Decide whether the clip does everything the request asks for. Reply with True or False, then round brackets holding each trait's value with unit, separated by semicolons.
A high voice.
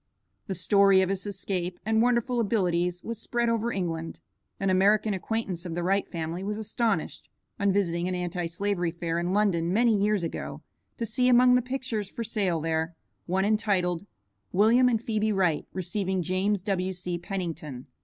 True (195 Hz)